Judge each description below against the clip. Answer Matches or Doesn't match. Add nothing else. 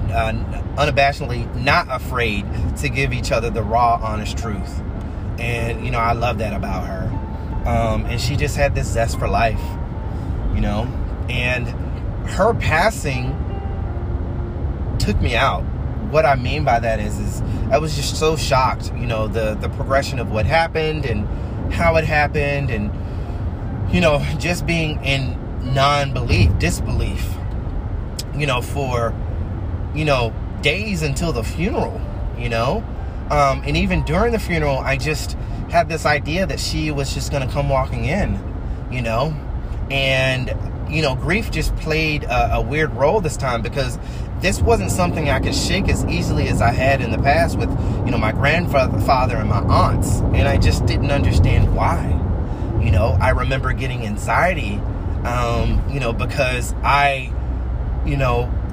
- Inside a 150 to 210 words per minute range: Matches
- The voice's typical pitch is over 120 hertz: Doesn't match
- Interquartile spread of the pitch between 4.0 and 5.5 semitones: Matches